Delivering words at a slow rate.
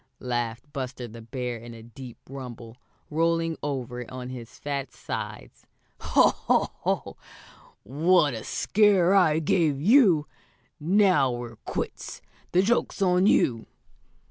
Yes: slow, 125 wpm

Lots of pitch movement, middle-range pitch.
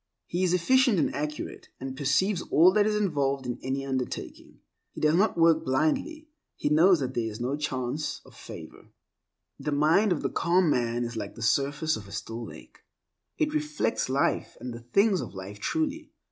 Yes: wide, 6.5 semitones; medium, 150 Hz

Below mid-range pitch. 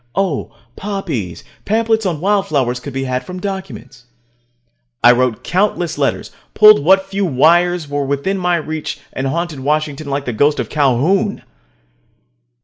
No: medium, 155 Hz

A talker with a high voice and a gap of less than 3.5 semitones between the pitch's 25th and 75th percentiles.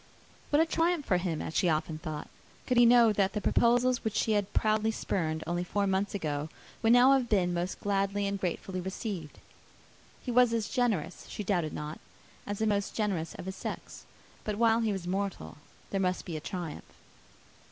No: high, 200 Hz; average, 4.1 semitones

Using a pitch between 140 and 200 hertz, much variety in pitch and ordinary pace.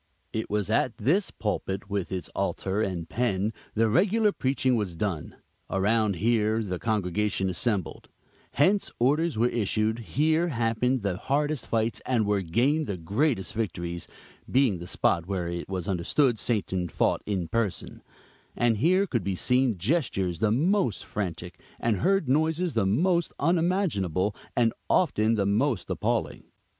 No: low, 110 Hz; wide, 5.9 semitones; average, 150 wpm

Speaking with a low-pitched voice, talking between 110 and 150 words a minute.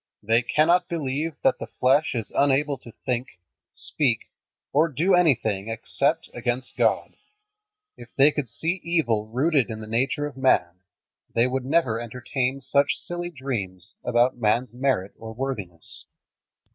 Yes: low, 130 Hz; average, 145 wpm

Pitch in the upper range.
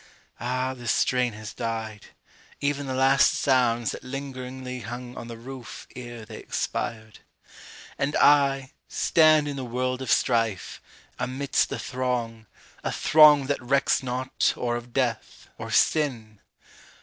No: low, 125 Hz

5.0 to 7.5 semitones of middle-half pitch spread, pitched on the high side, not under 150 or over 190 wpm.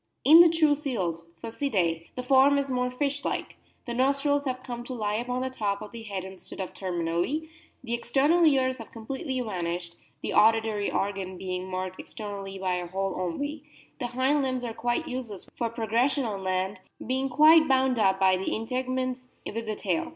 Yes: wide, 5.5 semitones; high, 235 Hz; average, 180 wpm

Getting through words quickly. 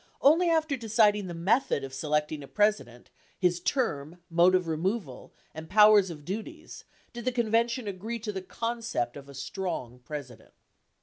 No: average, 160 wpm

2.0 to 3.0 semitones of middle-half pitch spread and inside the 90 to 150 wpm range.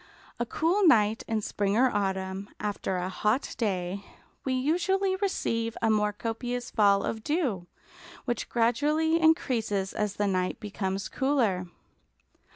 No: average, 5.0 semitones; slow, 135 wpm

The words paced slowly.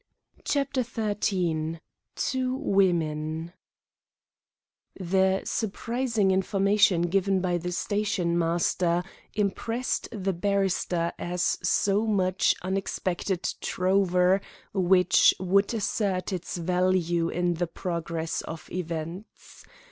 Yes: slow, 85 wpm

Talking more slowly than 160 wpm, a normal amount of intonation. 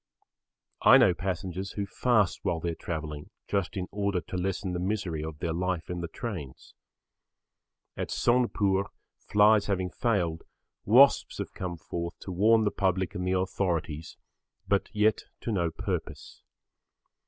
Yes: average, 150 wpm; average, 3.1 semitones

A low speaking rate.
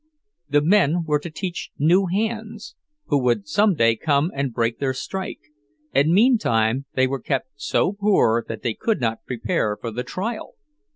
No: average, 170 wpm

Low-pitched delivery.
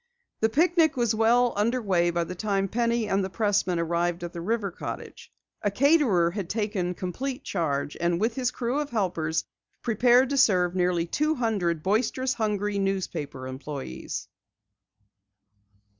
No: high, 200 Hz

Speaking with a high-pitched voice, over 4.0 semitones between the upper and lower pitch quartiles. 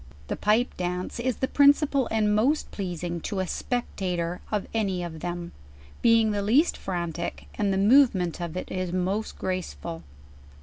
Yes: high, 195 Hz; average, 4.4 semitones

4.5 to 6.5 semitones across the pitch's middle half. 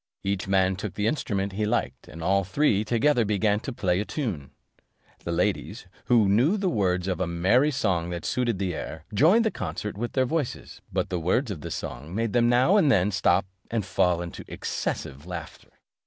Yes: average, 5.1 semitones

